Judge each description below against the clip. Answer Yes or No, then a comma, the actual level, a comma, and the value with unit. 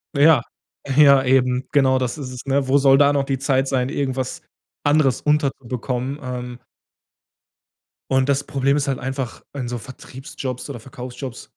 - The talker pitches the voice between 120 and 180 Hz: Yes, low, 135 Hz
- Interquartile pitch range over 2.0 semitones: No, narrow, 1.6 semitones